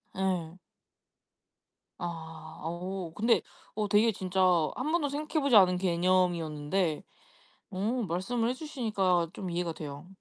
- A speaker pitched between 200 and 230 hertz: No, medium, 185 Hz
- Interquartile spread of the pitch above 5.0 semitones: No, average, 4.5 semitones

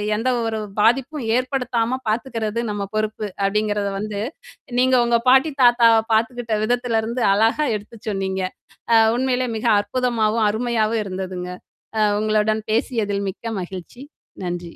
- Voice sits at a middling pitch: No, high, 220 Hz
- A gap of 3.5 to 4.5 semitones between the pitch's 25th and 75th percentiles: No, average, 2.7 semitones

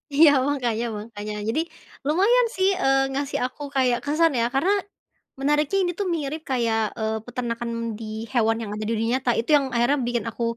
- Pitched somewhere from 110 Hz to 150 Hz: No, very high, 255 Hz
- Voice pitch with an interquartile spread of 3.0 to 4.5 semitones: Yes, average, 4.1 semitones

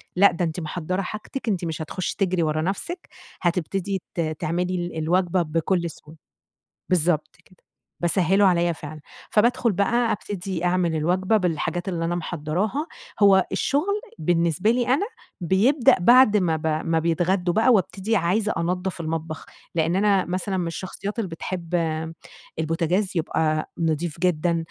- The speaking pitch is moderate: Yes, medium, 180 Hz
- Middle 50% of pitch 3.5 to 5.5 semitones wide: No, average, 3.1 semitones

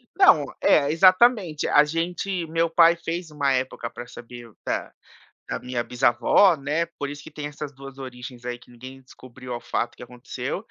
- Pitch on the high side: No, medium, 140 Hz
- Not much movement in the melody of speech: No, average, 5.0 semitones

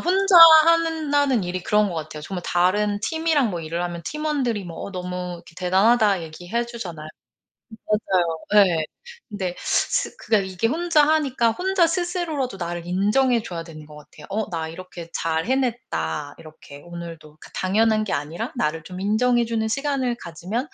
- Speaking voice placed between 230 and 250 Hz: No, high, 200 Hz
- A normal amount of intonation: No, wide, 7.0 semitones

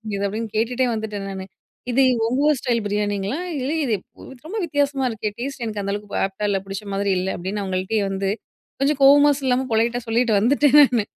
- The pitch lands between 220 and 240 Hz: Yes, high, 225 Hz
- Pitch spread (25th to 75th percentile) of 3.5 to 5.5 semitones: Yes, average, 4.7 semitones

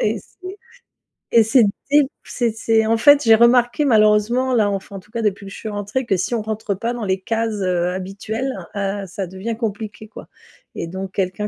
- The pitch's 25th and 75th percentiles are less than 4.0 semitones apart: Yes, average, 2.9 semitones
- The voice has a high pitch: Yes, high, 215 Hz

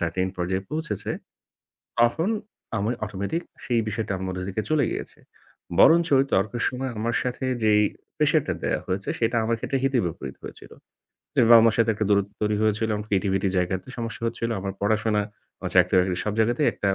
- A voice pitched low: Yes, low, 110 Hz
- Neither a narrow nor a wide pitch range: Yes, average, 3.4 semitones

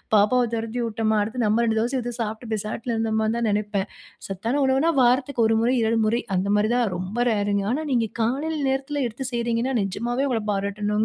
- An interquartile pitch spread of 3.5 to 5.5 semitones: No, average, 2.7 semitones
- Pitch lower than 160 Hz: No, high, 230 Hz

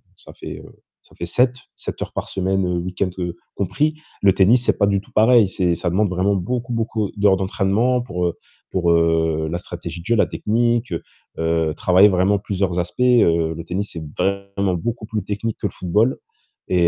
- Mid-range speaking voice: No, very low, 95 Hz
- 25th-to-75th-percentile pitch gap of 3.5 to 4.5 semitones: Yes, average, 3.8 semitones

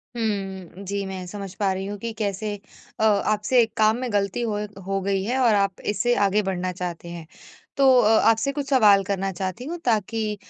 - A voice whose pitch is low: No, high, 205 Hz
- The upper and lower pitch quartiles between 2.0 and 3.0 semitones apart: Yes, average, 2.7 semitones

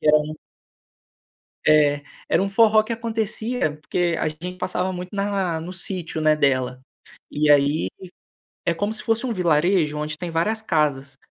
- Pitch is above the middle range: No, medium, 175 Hz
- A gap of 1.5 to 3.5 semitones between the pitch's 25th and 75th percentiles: No, average, 4.8 semitones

